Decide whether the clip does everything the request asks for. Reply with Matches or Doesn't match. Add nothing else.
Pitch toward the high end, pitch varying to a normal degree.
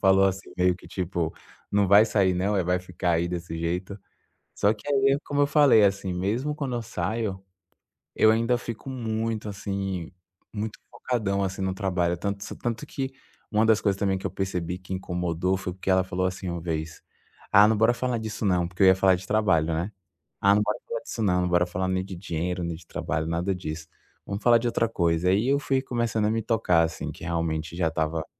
Doesn't match